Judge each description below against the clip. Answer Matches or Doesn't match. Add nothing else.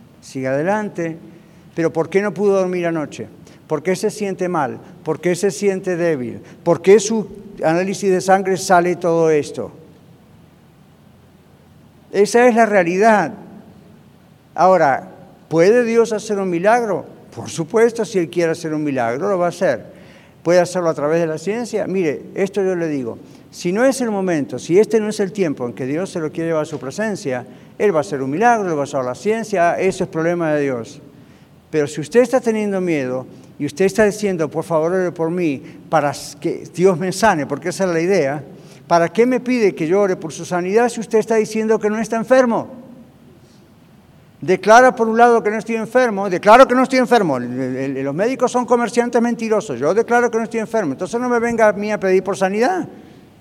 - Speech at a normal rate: Doesn't match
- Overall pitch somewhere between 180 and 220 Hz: Matches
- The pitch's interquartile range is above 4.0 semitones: Matches